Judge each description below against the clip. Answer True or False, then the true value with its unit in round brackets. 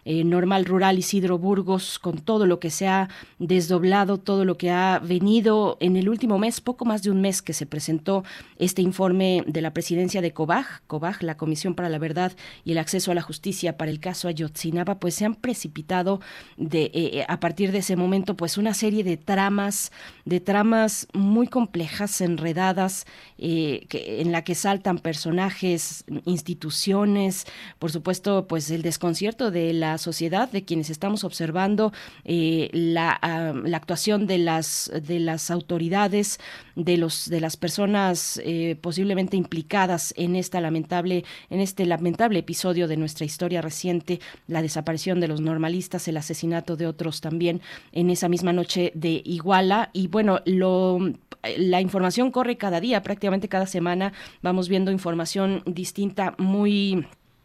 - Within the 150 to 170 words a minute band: True (160 wpm)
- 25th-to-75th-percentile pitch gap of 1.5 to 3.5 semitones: True (2.6 semitones)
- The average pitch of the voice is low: False (180 Hz)